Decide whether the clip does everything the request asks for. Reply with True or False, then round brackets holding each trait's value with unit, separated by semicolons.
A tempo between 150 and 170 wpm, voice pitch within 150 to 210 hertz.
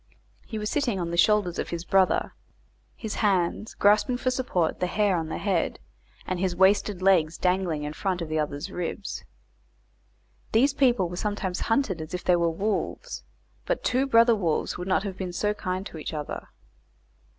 False (185 wpm; 190 Hz)